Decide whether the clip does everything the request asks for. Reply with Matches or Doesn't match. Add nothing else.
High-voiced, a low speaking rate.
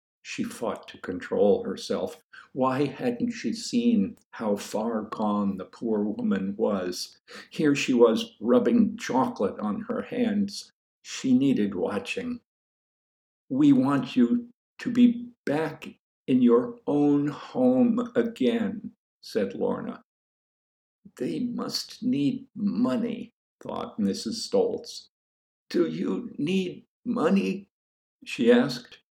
Matches